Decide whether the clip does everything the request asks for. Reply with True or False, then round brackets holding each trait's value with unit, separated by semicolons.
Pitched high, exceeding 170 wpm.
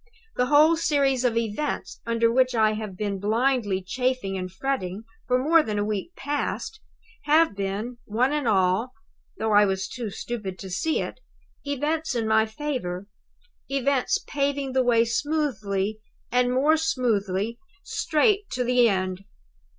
False (240 Hz; 150 wpm)